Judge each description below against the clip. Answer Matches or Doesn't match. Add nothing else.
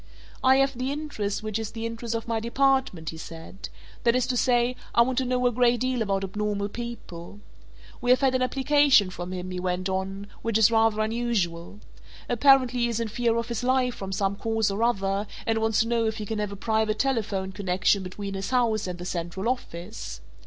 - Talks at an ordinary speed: Doesn't match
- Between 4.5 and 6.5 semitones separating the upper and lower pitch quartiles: Doesn't match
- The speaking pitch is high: Matches